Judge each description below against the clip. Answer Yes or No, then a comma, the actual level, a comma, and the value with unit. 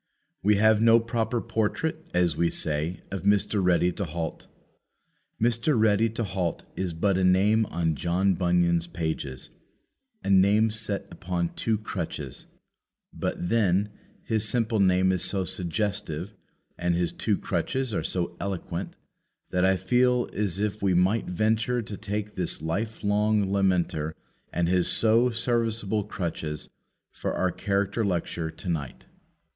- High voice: No, low, 100 Hz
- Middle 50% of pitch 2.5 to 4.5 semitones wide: Yes, average, 3.9 semitones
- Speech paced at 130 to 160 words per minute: Yes, average, 145 wpm